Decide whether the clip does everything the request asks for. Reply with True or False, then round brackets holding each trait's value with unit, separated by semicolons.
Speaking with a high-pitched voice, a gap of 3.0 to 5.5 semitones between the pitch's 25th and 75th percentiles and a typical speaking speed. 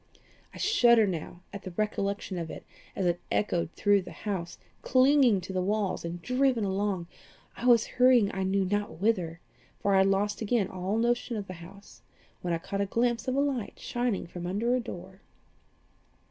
True (200 Hz; 4.2 semitones; 190 wpm)